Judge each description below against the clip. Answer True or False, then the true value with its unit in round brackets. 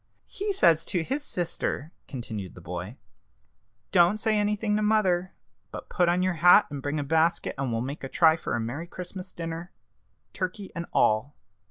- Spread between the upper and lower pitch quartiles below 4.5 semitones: False (5.1 semitones)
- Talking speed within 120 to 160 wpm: False (180 wpm)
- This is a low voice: False (170 Hz)